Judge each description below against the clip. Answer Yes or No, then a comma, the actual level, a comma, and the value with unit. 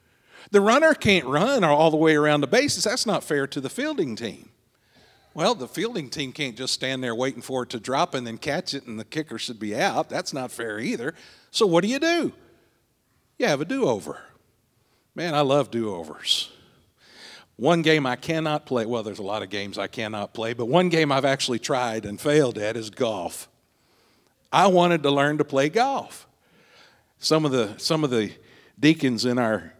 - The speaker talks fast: No, average, 195 wpm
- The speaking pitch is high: No, low, 135 Hz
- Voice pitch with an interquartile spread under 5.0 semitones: No, wide, 5.4 semitones